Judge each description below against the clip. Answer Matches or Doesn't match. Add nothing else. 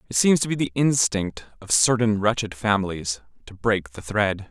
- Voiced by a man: Matches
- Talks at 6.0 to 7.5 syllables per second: Doesn't match